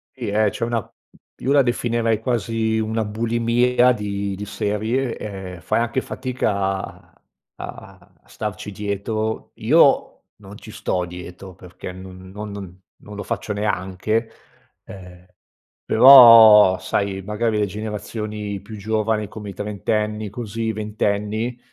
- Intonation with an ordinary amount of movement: No, narrow, 2.2 semitones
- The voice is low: Yes, low, 105 Hz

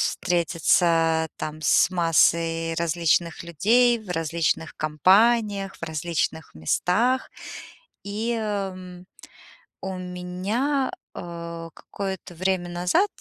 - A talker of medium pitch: Yes, medium, 180 Hz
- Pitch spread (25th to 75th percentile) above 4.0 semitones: No, average, 3.2 semitones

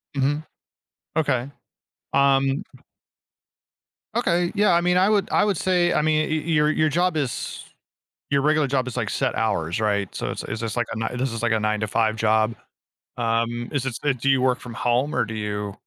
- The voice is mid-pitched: No, low, 130 Hz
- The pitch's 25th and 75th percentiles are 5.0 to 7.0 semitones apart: Yes, wide, 5.4 semitones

